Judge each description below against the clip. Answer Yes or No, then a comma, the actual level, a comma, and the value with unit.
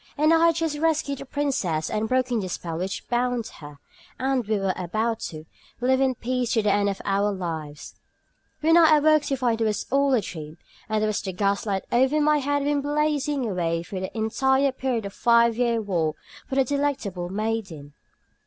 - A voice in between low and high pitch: No, high, 235 Hz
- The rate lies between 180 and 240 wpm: Yes, fast, 205 wpm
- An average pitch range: No, wide, 6.1 semitones